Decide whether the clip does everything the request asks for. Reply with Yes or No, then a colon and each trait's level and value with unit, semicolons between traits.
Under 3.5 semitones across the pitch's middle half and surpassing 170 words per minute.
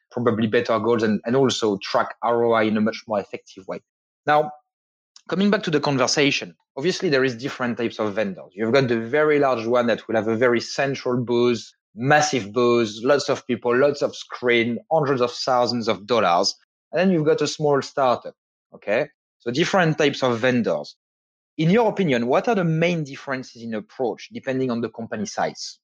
No: average, 4.2 semitones; average, 190 wpm